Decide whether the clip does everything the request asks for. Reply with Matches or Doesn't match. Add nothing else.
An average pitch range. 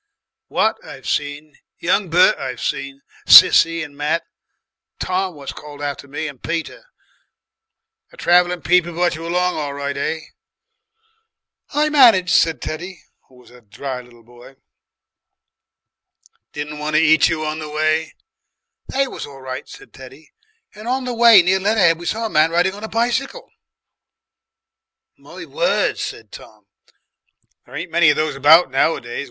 Matches